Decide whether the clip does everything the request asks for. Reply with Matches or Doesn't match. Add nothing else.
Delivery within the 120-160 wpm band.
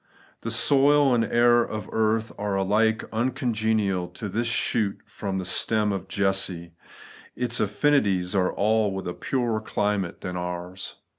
Matches